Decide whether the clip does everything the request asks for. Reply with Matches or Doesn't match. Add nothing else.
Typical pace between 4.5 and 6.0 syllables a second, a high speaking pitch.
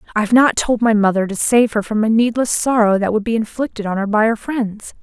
Matches